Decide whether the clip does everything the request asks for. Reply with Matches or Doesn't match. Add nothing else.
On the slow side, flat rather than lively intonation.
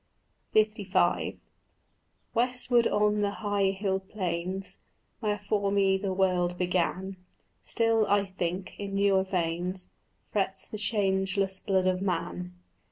Matches